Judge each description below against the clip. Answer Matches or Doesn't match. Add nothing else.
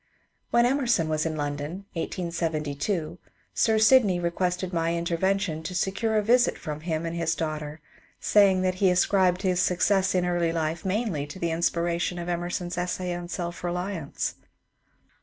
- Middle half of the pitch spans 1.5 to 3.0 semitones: Matches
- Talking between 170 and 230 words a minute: Doesn't match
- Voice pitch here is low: Doesn't match